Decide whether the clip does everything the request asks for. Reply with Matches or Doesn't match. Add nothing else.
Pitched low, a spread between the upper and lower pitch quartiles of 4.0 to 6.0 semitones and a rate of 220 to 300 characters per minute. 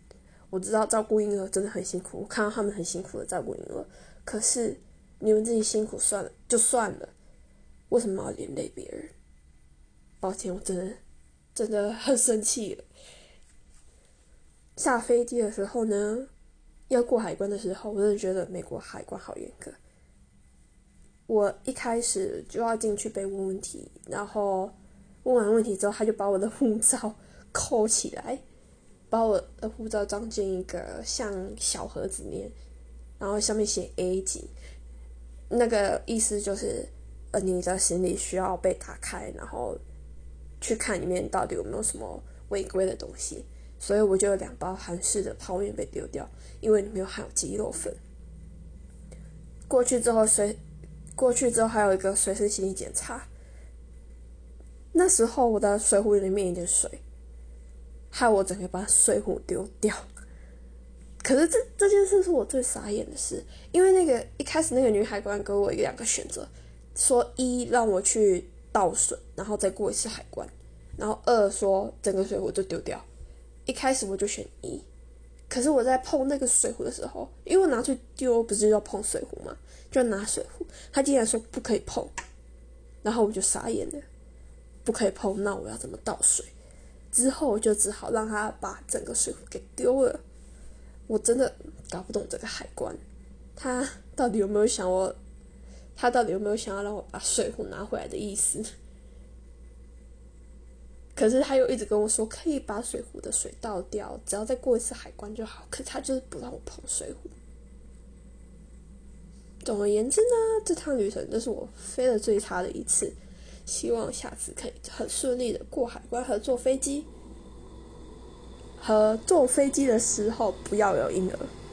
Doesn't match